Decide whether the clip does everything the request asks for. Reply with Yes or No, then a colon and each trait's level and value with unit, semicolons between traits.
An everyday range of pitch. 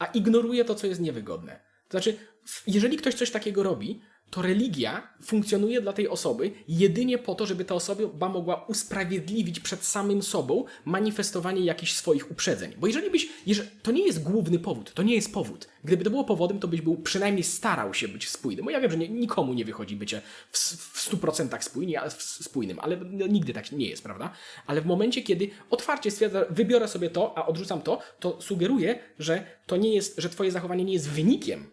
Yes: average, 3.7 semitones